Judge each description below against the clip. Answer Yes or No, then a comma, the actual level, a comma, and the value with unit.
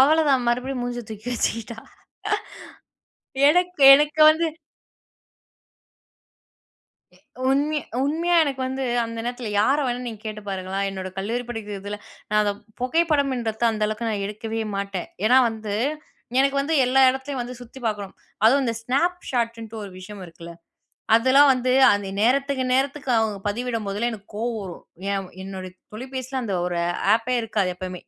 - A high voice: Yes, high, 235 Hz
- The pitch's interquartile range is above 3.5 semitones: Yes, average, 4.2 semitones